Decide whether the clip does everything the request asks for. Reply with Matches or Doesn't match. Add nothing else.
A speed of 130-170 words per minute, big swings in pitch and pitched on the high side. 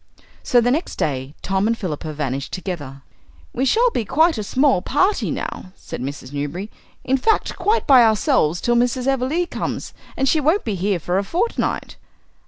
Doesn't match